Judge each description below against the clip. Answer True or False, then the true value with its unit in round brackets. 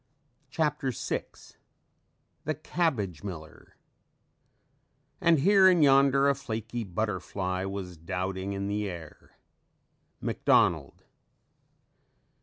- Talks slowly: True (85 wpm)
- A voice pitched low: True (105 Hz)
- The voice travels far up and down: True (7.0 semitones)